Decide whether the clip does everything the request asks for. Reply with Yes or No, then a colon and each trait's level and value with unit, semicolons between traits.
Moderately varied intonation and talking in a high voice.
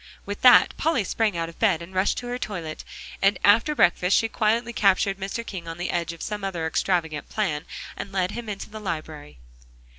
Yes: average, 4.2 semitones; high, 195 Hz